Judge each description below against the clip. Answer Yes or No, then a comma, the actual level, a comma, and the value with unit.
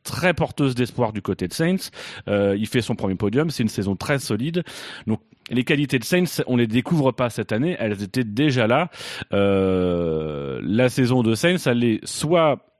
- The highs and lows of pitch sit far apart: Yes, wide, 6.1 semitones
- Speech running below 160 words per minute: No, average, 195 wpm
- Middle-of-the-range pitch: No, low, 125 Hz